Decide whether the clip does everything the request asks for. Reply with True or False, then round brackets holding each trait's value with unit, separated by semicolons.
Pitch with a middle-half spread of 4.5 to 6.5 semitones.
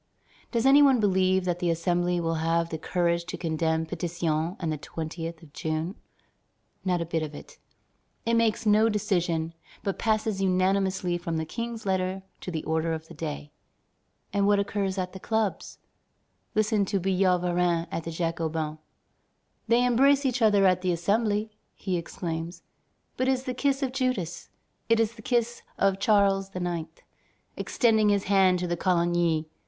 False (4.1 semitones)